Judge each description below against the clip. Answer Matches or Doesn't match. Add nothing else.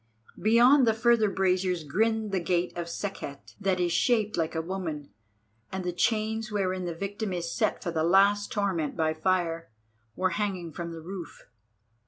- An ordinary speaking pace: Matches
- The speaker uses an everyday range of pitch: Matches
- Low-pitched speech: Doesn't match